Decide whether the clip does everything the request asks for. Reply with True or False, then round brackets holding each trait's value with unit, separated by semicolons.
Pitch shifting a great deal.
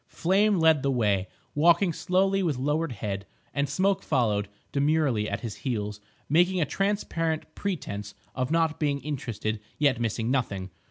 True (6.6 semitones)